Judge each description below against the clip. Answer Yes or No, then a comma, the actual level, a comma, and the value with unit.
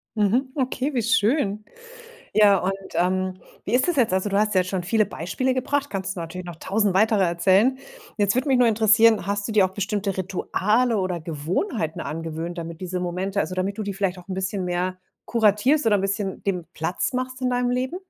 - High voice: Yes, high, 200 Hz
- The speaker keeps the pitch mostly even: No, average, 3.9 semitones